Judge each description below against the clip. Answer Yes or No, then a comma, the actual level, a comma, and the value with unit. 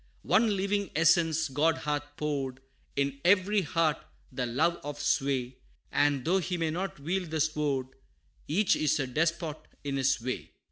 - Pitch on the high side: No, medium, 155 Hz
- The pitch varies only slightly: No, average, 3.7 semitones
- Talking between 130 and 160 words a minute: Yes, average, 155 wpm